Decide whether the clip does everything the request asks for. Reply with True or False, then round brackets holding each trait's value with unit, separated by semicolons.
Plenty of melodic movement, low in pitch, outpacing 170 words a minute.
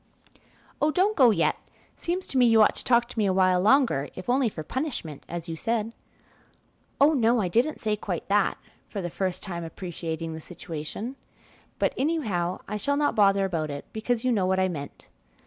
False (6.1 semitones; 205 Hz; 200 wpm)